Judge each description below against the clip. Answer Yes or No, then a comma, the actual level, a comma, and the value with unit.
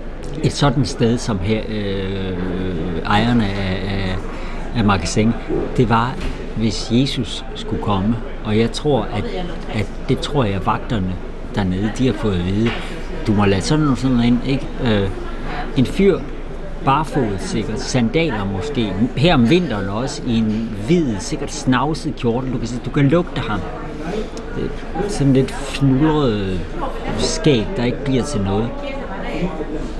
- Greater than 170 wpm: No, average, 150 wpm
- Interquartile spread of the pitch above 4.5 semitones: Yes, average, 5.1 semitones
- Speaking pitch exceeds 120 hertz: No, low, 115 Hz